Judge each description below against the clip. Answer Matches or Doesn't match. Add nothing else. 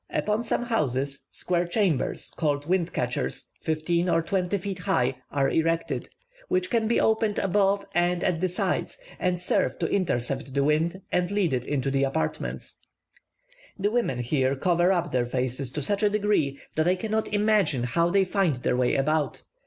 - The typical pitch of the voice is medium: Matches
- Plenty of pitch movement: Matches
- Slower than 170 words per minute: Doesn't match